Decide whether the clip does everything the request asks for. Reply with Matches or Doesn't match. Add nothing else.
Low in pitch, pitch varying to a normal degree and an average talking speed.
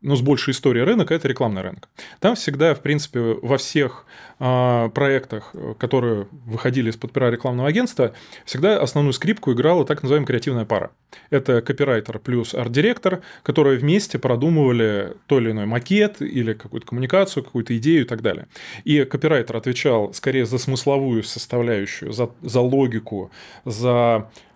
Matches